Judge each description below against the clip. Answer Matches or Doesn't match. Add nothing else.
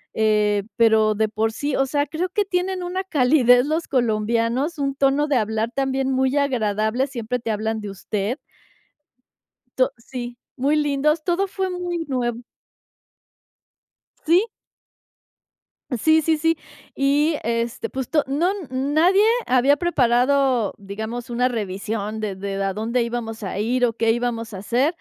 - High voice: Matches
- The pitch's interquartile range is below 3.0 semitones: Doesn't match